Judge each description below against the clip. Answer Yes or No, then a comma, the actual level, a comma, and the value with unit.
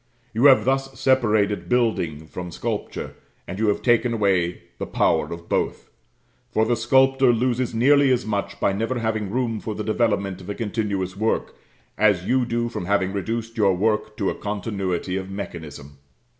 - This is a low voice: Yes, low, 110 Hz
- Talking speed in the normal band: Yes, average, 170 wpm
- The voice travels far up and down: No, average, 3.4 semitones